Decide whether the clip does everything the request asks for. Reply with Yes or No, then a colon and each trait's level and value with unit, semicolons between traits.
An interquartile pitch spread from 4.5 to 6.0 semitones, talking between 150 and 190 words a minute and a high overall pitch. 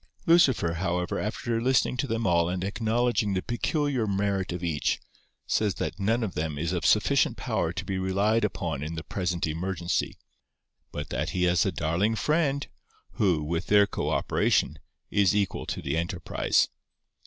No: average, 4.8 semitones; average, 165 wpm; very low, 95 Hz